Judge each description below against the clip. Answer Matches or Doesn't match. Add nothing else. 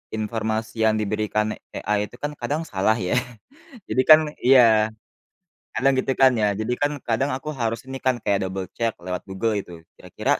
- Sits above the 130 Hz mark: Doesn't match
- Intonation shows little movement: Doesn't match